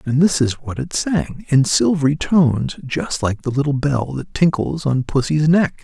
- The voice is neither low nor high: Yes, medium, 145 Hz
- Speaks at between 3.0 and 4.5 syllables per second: Yes, 4.4 syllables/s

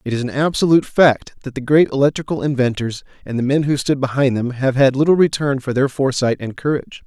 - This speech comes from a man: Yes, male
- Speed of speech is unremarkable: No, fast, 220 wpm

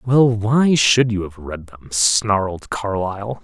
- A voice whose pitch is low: Yes, low, 105 Hz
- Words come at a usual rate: Yes, average, 155 wpm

